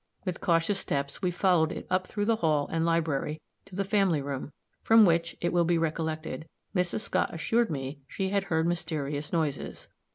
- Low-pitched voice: No, medium, 165 Hz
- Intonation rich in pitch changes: No, average, 3.1 semitones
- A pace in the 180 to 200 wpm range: Yes, average, 185 wpm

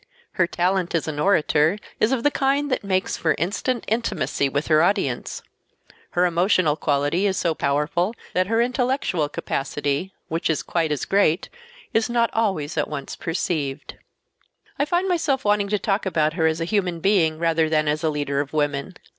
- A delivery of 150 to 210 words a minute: Yes, average, 180 wpm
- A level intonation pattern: No, average, 5.1 semitones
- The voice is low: No, medium, 175 Hz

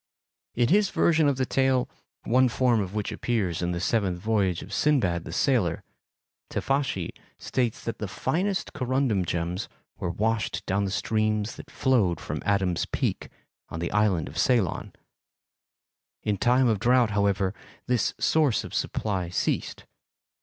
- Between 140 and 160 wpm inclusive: Yes, average, 150 wpm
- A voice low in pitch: Yes, low, 110 Hz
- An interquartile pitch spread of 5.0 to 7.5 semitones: Yes, wide, 5.4 semitones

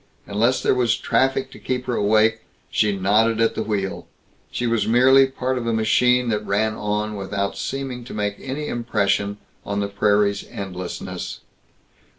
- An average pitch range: Yes, average, 3.4 semitones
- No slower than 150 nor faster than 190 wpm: Yes, average, 165 wpm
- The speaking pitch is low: Yes, low, 110 Hz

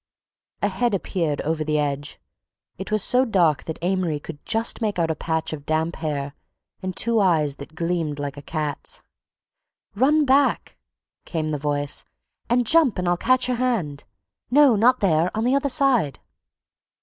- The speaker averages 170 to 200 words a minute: No, average, 160 wpm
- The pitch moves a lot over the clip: Yes, wide, 7.5 semitones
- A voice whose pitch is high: No, medium, 175 Hz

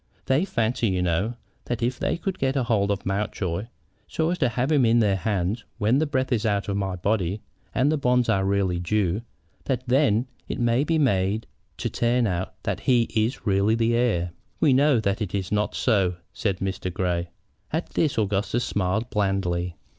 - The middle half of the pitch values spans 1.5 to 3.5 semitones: No, average, 4.3 semitones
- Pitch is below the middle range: Yes, low, 110 Hz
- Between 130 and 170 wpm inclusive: No, average, 195 wpm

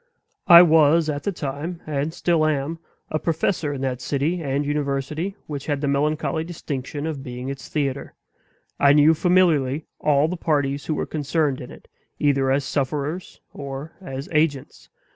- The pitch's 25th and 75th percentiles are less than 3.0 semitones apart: Yes, narrow, 2.6 semitones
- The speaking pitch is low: No, medium, 145 Hz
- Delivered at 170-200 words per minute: No, average, 160 wpm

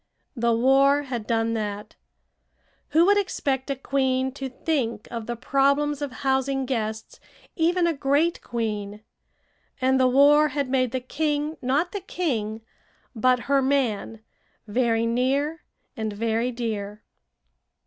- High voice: Yes, very high, 260 Hz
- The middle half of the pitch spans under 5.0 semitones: Yes, average, 3.8 semitones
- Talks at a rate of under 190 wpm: Yes, slow, 135 wpm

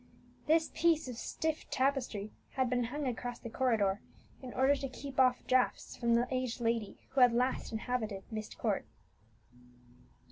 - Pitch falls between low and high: No, very high, 250 Hz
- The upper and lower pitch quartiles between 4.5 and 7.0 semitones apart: No, narrow, 2.4 semitones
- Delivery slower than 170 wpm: Yes, average, 155 wpm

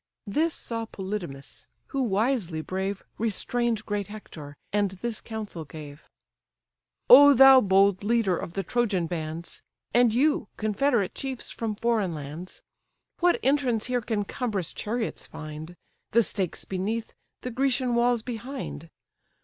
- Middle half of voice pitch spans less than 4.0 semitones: No, average, 4.7 semitones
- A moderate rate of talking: No, slow, 130 wpm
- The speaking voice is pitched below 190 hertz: No, high, 215 Hz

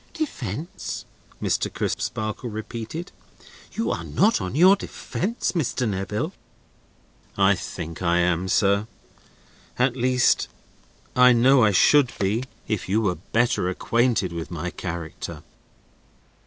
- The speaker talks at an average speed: No, slow, 115 wpm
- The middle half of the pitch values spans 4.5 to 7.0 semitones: Yes, wide, 5.5 semitones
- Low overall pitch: Yes, low, 110 Hz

